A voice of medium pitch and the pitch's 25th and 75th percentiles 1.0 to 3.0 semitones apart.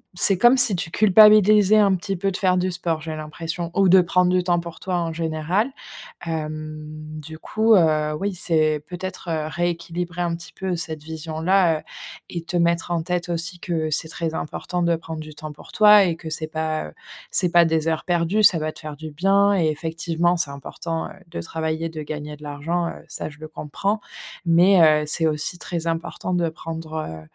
Yes: medium, 165 Hz; narrow, 2.4 semitones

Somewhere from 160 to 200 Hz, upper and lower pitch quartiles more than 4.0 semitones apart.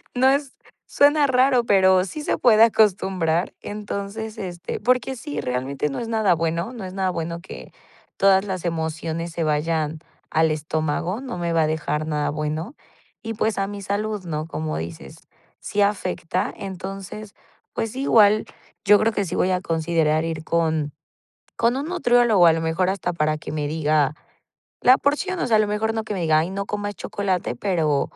Yes: medium, 185 Hz; average, 5.1 semitones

